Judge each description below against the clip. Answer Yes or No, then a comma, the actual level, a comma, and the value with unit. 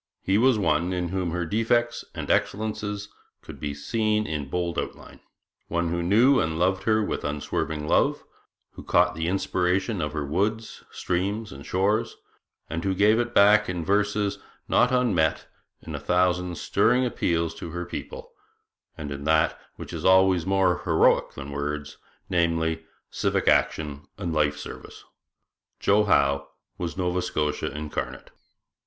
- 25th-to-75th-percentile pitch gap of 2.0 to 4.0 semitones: No, average, 4.6 semitones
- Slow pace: No, average, 150 wpm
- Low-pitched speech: Yes, very low, 90 Hz